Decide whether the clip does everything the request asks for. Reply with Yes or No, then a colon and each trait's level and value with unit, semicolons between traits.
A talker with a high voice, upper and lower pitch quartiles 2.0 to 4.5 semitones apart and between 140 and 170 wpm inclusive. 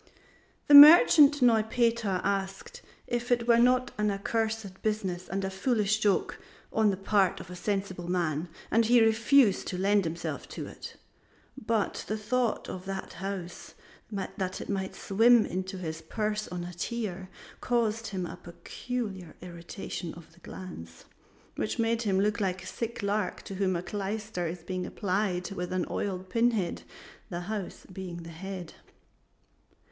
Yes: high, 195 Hz; average, 3.5 semitones; average, 150 wpm